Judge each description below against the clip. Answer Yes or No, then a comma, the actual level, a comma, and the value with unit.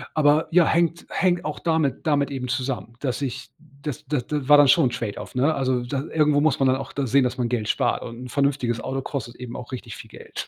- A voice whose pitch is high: No, low, 135 Hz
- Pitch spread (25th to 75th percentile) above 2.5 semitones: Yes, average, 2.9 semitones